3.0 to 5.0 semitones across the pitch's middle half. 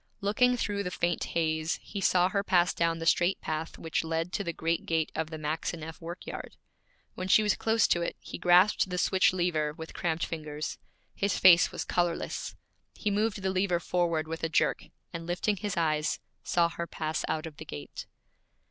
No: narrow, 2.6 semitones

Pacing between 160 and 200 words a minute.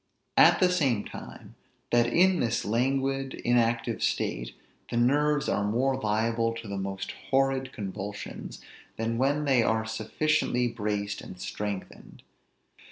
No: slow, 135 wpm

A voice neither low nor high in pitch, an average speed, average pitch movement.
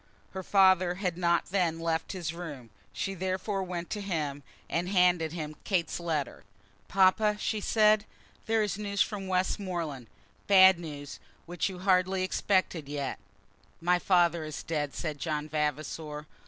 Yes: medium, 175 Hz; average, 145 wpm; average, 3.3 semitones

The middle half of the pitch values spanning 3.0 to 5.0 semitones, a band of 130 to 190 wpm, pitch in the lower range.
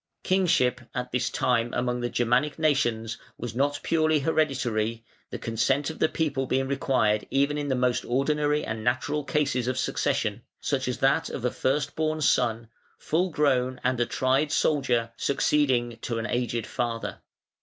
Yes: average, 3.4 semitones; average, 165 wpm; low, 130 Hz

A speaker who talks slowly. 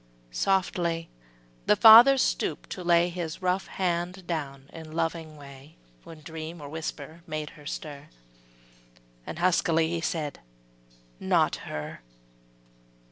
Yes: slow, 120 wpm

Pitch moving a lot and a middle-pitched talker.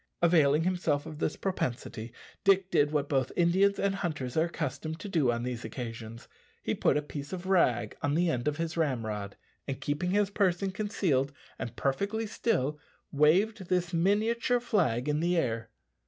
Yes: wide, 6.1 semitones; medium, 160 Hz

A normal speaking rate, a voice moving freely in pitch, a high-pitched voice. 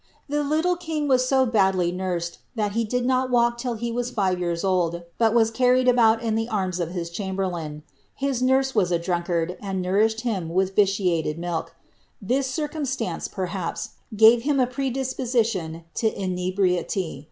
Yes: average, 165 wpm; wide, 5.7 semitones; high, 215 Hz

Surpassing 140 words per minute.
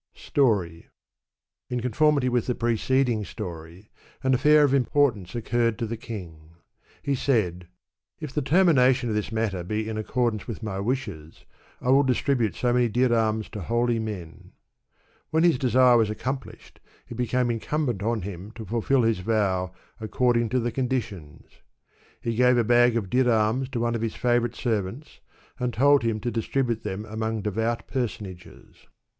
Yes: average, 165 wpm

